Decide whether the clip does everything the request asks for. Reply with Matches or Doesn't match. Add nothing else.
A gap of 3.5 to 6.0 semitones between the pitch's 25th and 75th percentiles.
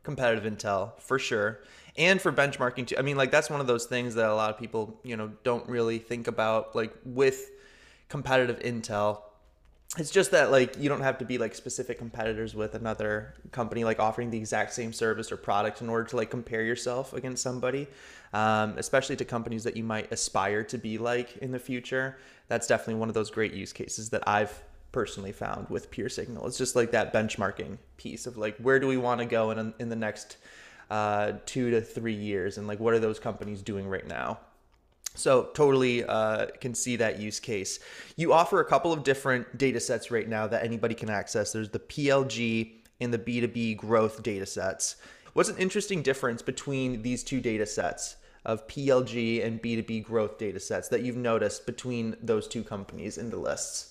Doesn't match